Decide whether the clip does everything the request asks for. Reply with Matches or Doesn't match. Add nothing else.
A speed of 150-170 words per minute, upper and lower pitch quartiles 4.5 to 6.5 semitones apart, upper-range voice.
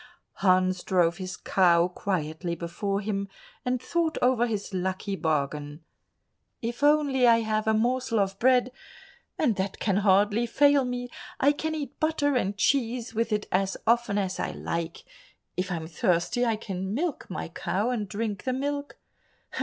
Matches